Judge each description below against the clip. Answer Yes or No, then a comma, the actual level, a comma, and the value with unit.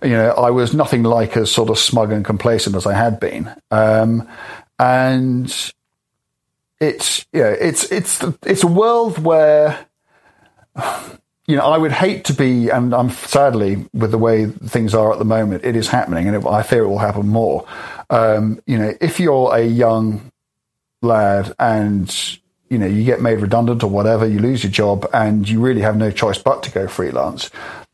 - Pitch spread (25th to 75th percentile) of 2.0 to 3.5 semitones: Yes, average, 2.9 semitones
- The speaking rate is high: No, average, 185 wpm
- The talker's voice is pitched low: Yes, low, 115 Hz